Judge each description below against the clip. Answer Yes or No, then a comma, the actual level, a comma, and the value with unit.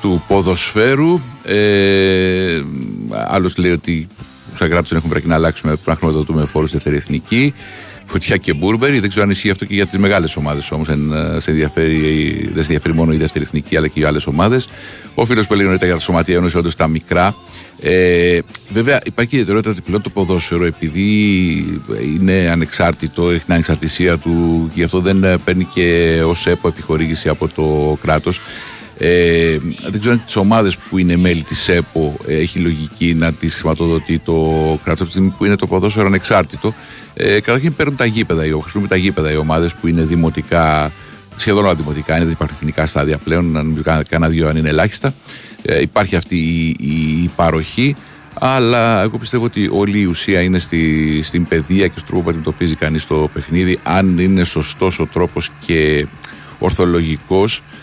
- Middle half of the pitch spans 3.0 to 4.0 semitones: Yes, average, 3.7 semitones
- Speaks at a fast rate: Yes, fast, 180 wpm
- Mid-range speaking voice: No, very low, 85 Hz